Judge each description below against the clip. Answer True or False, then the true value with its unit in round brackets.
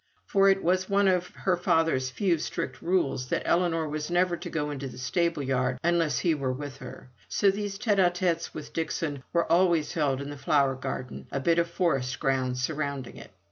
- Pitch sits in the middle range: True (160 Hz)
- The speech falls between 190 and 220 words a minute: True (205 wpm)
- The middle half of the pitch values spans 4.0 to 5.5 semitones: True (4.7 semitones)